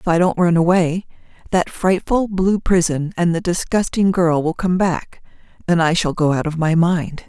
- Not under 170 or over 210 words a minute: Yes, average, 200 wpm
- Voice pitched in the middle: Yes, medium, 175 Hz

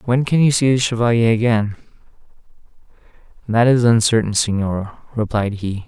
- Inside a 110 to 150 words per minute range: Yes, slow, 135 wpm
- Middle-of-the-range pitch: No, low, 115 Hz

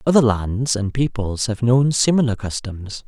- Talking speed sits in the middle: Yes, average, 155 wpm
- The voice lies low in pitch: Yes, low, 115 Hz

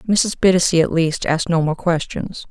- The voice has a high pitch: No, medium, 170 Hz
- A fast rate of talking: No, average, 190 wpm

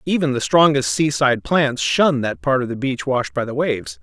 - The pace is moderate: No, fast, 225 wpm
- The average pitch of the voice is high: No, low, 135 Hz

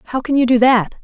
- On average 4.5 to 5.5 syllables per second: No, 6.9 syllables/s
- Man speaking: No, female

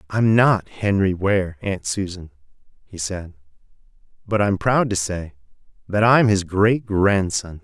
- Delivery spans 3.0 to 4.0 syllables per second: Yes, 3.9 syllables/s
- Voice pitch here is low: Yes, very low, 95 Hz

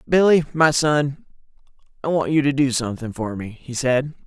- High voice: No, medium, 140 Hz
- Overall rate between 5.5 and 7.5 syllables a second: No, 5.1 syllables/s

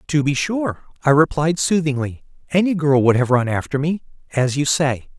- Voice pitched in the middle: Yes, medium, 150 Hz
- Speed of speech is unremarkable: Yes, average, 185 wpm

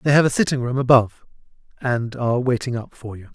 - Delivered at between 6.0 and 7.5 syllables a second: Yes, 6.2 syllables/s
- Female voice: No, male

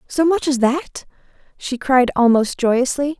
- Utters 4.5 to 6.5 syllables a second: No, 4.0 syllables/s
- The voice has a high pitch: Yes, very high, 265 Hz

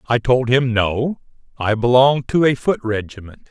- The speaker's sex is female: No, male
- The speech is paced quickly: No, average, 170 wpm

